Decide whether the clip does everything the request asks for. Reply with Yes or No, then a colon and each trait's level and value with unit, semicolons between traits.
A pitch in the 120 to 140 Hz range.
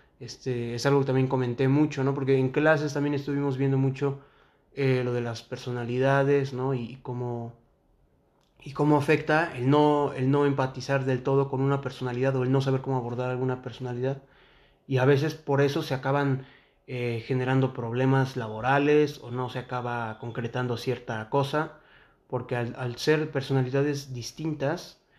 Yes: low, 135 Hz